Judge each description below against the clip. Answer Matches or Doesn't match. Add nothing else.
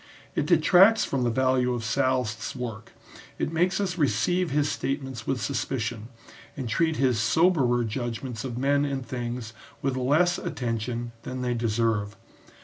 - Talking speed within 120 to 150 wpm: Matches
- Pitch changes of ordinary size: Matches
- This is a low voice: Matches